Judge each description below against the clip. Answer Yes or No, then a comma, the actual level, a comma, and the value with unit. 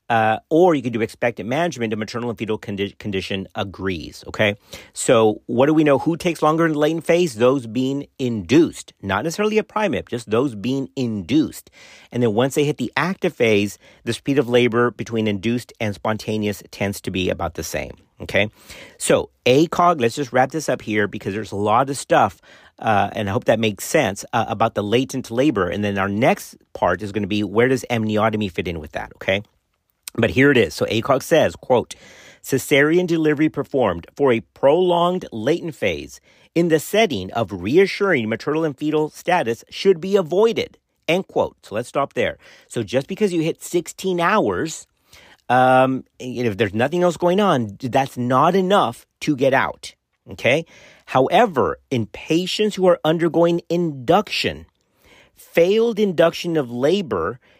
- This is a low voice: Yes, low, 130 Hz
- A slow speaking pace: No, average, 175 wpm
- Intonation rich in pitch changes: Yes, wide, 7.1 semitones